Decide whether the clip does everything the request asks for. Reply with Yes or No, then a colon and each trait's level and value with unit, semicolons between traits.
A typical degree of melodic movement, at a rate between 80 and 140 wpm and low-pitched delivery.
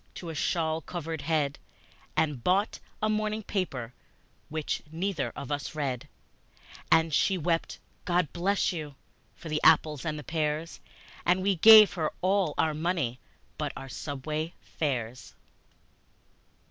No: average, 3.4 semitones; slow, 135 wpm; medium, 160 Hz